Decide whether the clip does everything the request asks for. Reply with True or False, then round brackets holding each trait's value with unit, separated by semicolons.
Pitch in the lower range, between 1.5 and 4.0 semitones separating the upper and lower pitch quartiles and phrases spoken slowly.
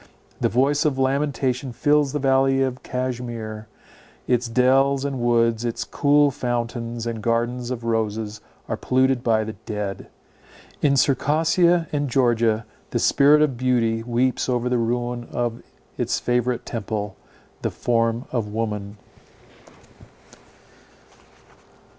True (120 Hz; 2.6 semitones; 120 wpm)